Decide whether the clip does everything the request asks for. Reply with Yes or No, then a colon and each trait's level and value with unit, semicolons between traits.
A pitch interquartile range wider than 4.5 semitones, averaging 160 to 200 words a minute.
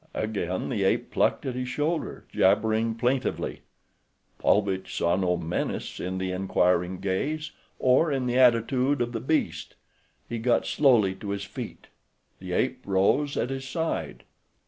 No: wide, 5.6 semitones; average, 145 wpm